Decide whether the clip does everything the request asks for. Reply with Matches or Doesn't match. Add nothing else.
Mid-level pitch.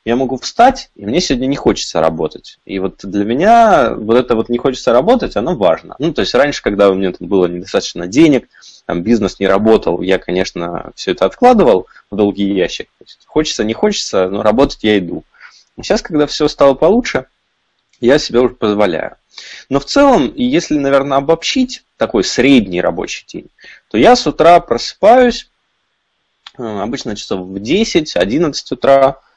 Doesn't match